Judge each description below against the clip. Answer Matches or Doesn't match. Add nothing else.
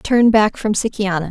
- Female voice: Matches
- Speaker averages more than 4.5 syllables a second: Matches